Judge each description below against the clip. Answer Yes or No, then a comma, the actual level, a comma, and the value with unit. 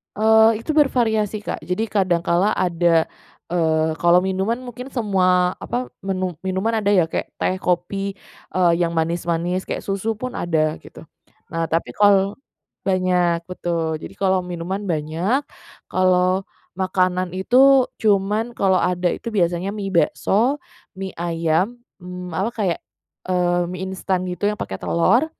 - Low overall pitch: No, medium, 185 Hz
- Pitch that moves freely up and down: No, average, 2.8 semitones